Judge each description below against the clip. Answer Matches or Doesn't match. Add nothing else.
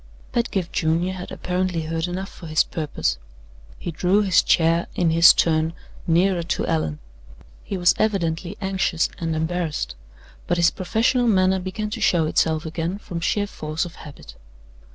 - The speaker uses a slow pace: Doesn't match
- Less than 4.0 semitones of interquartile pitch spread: Matches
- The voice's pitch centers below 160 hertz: Doesn't match